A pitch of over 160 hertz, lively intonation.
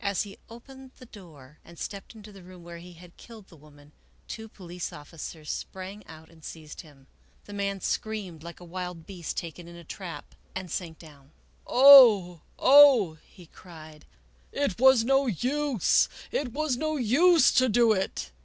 Yes: medium, 185 Hz; wide, 6.2 semitones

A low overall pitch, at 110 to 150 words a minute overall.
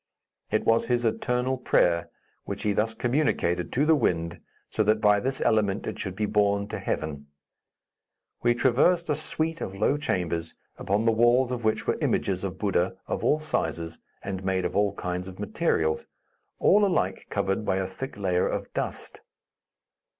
No: low, 105 Hz; average, 170 wpm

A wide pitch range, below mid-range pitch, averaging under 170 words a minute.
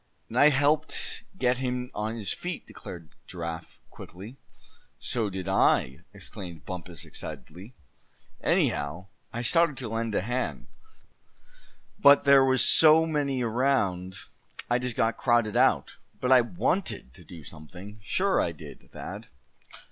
Yes: wide, 6.4 semitones; low, 115 Hz; slow, 135 wpm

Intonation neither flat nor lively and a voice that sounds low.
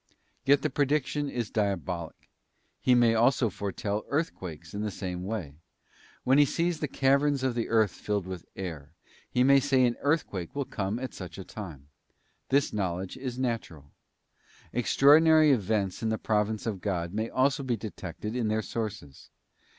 No: wide, 5.7 semitones; low, 110 Hz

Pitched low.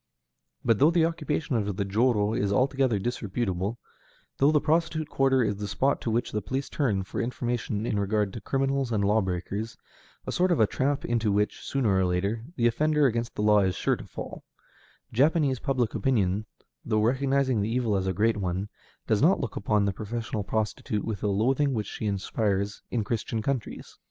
Yes: low, 110 Hz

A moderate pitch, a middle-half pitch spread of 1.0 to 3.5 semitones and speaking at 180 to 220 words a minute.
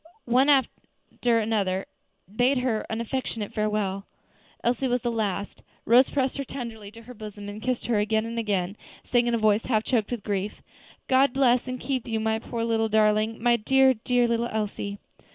No: high, 230 Hz; narrow, 2.6 semitones; average, 185 wpm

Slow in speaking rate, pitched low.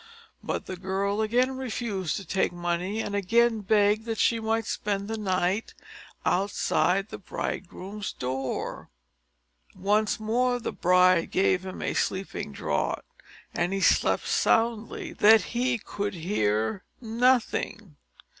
No: slow, 130 wpm; high, 205 Hz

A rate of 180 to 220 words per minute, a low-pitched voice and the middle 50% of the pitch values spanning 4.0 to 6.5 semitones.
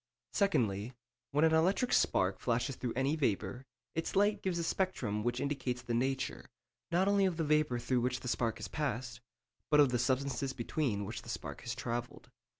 Yes: average, 185 wpm; low, 130 Hz; average, 4.9 semitones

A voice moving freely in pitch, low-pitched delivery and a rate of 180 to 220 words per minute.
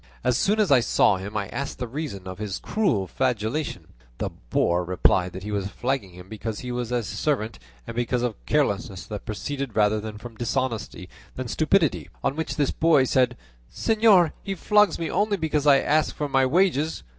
Yes: wide, 6.4 semitones; low, 125 Hz; average, 190 wpm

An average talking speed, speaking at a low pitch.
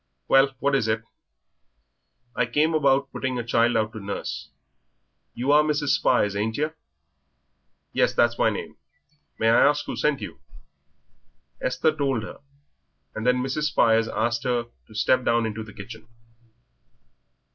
Yes: average, 150 wpm; low, 120 Hz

